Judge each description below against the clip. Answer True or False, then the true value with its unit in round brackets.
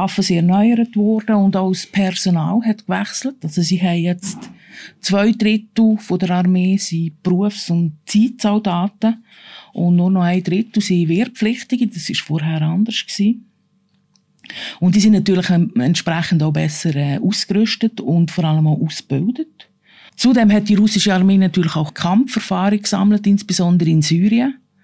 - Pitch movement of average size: True (3.5 semitones)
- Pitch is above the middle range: True (195 Hz)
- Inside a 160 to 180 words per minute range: False (145 wpm)